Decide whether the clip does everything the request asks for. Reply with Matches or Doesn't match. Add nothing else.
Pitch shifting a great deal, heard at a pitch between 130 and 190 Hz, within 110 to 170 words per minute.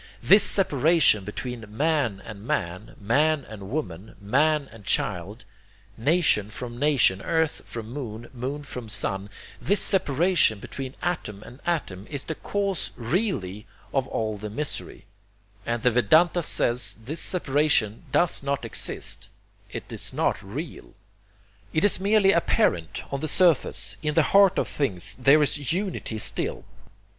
Matches